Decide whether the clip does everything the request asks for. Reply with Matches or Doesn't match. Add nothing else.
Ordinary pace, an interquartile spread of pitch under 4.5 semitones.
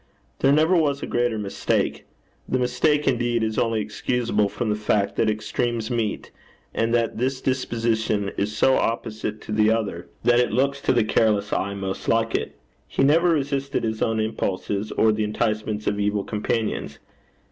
Matches